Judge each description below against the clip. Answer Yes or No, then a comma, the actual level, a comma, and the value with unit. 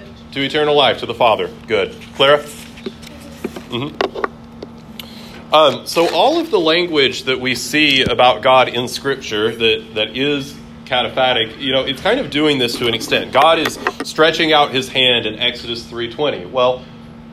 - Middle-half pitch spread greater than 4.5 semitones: No, average, 3.7 semitones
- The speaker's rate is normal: Yes, average, 165 wpm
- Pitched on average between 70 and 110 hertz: No, low, 130 Hz